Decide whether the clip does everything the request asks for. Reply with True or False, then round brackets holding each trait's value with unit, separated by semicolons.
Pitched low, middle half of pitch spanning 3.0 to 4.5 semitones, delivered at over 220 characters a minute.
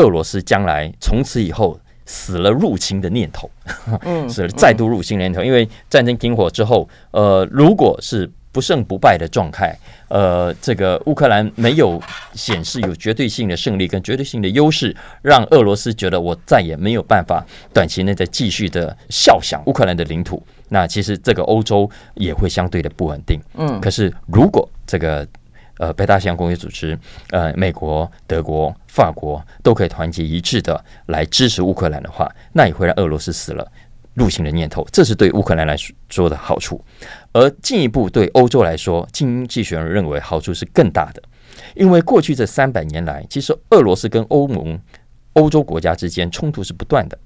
False (95 Hz; 5.5 semitones; 285 characters per minute)